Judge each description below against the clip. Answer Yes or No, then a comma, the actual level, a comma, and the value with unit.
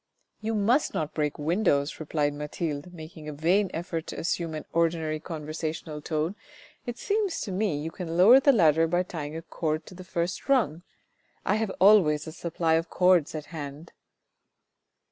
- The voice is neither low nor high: Yes, medium, 165 Hz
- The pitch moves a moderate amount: Yes, average, 3.1 semitones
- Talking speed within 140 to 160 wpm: No, average, 175 wpm